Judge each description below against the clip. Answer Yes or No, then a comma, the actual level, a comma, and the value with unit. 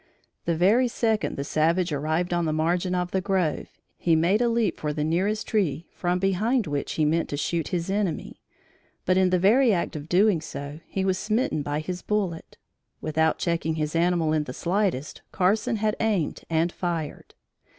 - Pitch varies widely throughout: No, average, 3.8 semitones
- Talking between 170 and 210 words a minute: Yes, average, 185 wpm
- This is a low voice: No, medium, 175 Hz